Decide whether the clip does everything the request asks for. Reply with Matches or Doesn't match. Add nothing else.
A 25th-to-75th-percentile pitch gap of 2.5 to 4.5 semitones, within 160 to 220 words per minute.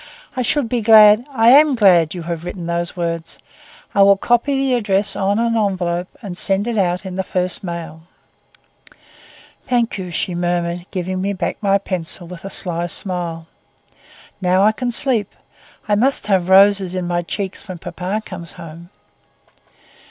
Matches